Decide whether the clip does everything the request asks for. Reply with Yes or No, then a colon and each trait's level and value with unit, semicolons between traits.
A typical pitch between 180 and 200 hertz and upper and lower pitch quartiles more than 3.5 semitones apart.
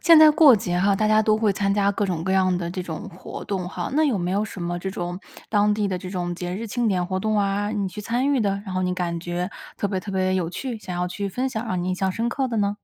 No: high, 195 Hz; average, 2.9 semitones